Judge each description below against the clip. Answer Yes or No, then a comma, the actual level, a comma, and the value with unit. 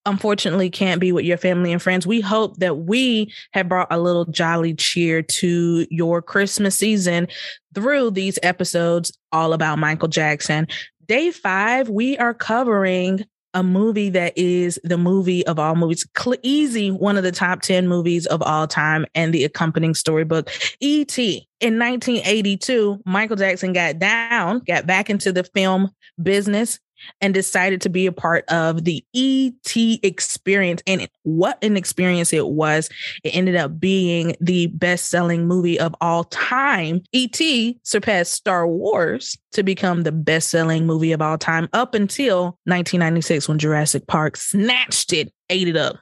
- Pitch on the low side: No, medium, 180 Hz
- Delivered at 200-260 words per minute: No, average, 160 wpm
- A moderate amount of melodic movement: Yes, average, 3.4 semitones